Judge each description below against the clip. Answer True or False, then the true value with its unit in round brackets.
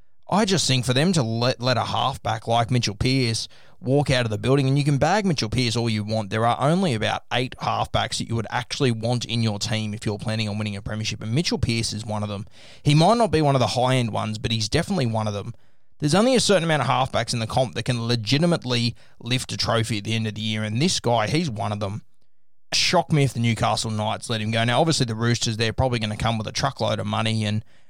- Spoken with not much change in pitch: False (3.4 semitones)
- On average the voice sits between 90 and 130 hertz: True (120 Hz)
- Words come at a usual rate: False (265 wpm)